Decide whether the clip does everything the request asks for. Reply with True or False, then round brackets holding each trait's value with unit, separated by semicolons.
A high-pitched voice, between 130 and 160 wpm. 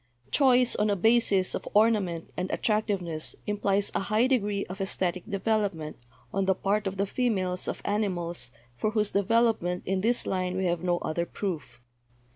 False (195 Hz; 170 wpm)